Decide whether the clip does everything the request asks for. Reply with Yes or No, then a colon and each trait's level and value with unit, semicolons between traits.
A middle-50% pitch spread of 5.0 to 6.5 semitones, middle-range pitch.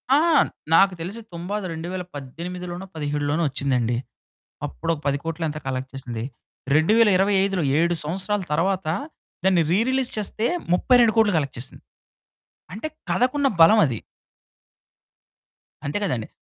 Yes: wide, 5.4 semitones; medium, 175 Hz